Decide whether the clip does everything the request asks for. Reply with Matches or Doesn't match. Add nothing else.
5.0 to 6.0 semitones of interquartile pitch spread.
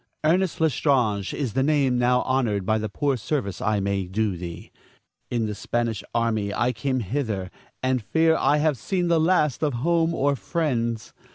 Matches